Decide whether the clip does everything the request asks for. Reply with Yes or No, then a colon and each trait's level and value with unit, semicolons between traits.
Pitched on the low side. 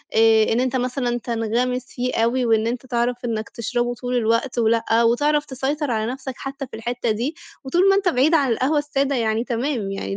No: high, 245 Hz